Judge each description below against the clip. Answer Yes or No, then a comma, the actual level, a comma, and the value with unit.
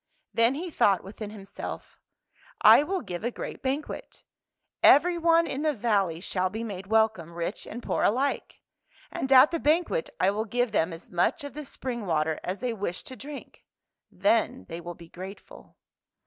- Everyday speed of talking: Yes, average, 175 wpm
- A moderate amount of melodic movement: No, wide, 7.0 semitones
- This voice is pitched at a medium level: No, high, 225 Hz